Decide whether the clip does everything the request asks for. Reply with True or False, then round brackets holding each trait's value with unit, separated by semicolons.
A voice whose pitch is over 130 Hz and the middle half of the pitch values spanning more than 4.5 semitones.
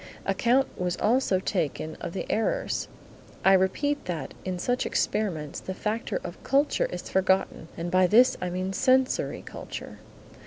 True (190 Hz; 5.6 semitones)